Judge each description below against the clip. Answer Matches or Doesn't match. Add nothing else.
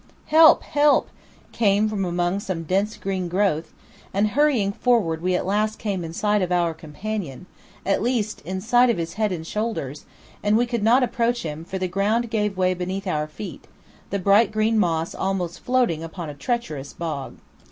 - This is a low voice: Doesn't match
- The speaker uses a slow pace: Doesn't match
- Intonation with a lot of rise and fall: Doesn't match